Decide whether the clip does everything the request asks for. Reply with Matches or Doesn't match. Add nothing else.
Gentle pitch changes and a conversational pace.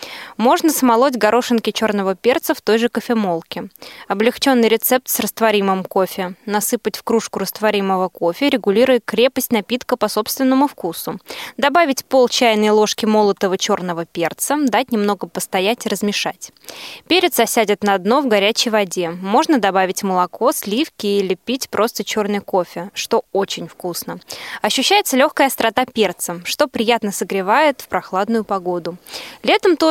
Doesn't match